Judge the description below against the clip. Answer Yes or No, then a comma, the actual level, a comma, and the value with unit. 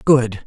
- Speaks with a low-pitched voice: Yes, low, 125 Hz